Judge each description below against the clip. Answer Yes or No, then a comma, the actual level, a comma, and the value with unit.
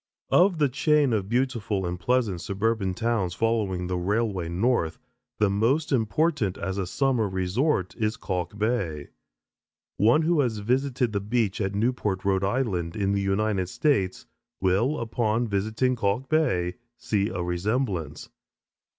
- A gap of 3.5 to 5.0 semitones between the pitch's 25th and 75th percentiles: Yes, average, 4.7 semitones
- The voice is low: Yes, low, 105 Hz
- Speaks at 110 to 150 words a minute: Yes, average, 140 wpm